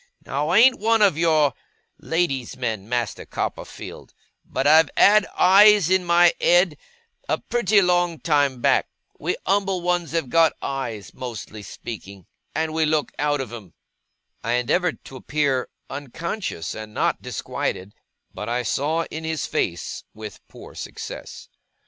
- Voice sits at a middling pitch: Yes, medium, 150 Hz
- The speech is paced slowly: No, average, 145 wpm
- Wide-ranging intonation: Yes, wide, 6.3 semitones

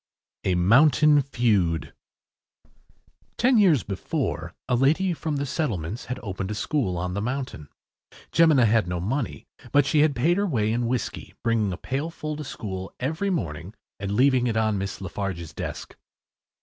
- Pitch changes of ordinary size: No, wide, 7.1 semitones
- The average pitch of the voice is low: Yes, low, 120 Hz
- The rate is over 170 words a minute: No, average, 160 wpm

